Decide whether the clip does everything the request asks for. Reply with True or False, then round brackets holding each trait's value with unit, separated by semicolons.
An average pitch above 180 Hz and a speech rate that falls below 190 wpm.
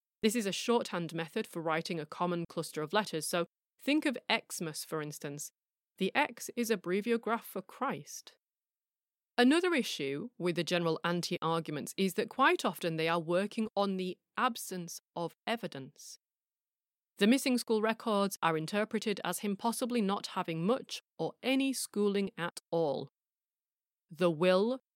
True (190 Hz; 150 wpm)